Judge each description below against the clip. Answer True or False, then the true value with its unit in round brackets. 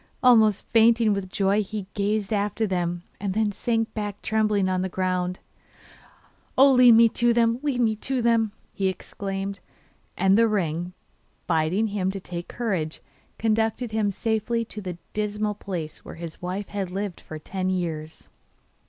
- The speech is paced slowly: False (155 wpm)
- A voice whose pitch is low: False (205 Hz)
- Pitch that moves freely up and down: False (3.2 semitones)